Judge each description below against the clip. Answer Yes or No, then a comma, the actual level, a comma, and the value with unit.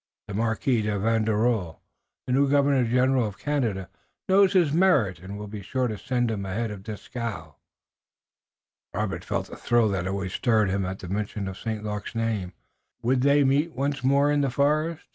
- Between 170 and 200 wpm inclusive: Yes, average, 180 wpm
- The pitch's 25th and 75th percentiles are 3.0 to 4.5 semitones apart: No, average, 5.1 semitones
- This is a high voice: No, low, 115 Hz